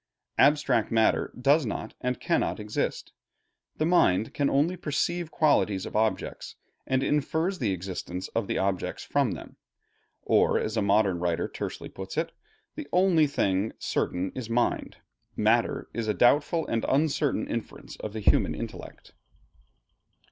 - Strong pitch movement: Yes, wide, 6.9 semitones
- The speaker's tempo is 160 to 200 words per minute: No, average, 145 wpm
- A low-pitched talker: Yes, low, 120 Hz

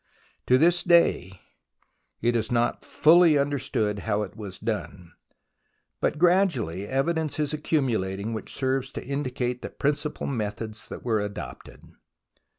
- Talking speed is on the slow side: Yes, slow, 130 wpm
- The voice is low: Yes, low, 125 Hz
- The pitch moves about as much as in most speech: No, wide, 5.9 semitones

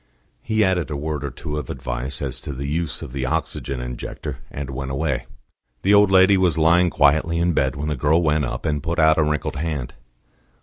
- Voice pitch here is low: Yes, very low, 75 Hz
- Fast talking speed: Yes, fast, 215 wpm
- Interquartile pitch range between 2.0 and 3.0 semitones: No, average, 3.4 semitones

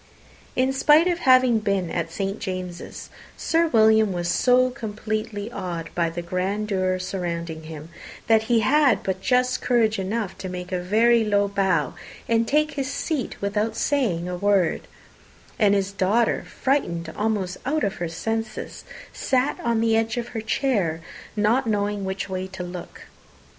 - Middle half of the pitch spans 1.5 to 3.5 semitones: No, average, 4.3 semitones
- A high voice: Yes, high, 210 Hz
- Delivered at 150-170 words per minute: Yes, average, 160 wpm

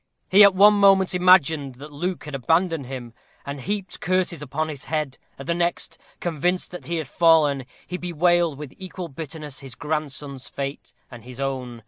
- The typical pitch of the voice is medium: Yes, medium, 155 Hz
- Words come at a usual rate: Yes, average, 175 wpm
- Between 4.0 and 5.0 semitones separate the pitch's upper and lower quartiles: Yes, average, 4.5 semitones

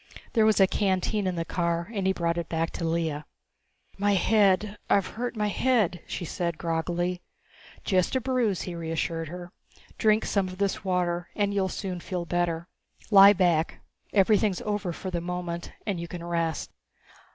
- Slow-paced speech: No, average, 175 wpm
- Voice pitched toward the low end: No, medium, 180 Hz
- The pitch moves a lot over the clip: No, average, 2.9 semitones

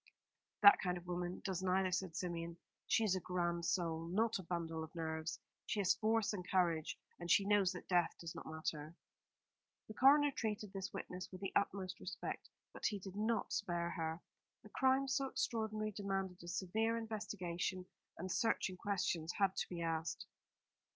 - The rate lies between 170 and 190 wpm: Yes, average, 175 wpm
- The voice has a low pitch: No, medium, 185 Hz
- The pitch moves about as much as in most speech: Yes, average, 3.3 semitones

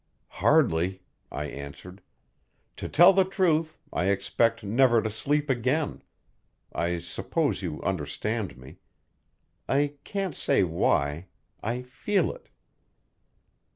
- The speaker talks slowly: Yes, slow, 110 wpm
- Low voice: Yes, low, 115 Hz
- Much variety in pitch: Yes, wide, 8.8 semitones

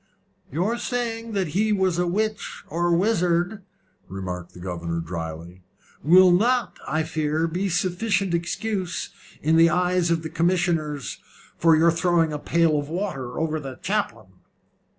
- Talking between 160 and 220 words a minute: No, average, 145 wpm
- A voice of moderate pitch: Yes, medium, 170 Hz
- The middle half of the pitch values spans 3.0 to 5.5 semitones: Yes, average, 3.9 semitones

